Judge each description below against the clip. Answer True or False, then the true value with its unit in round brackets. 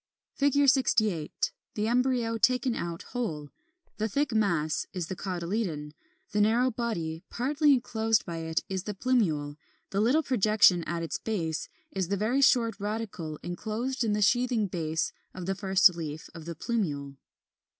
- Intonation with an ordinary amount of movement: False (5.9 semitones)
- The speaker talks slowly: False (150 wpm)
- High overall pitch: True (210 Hz)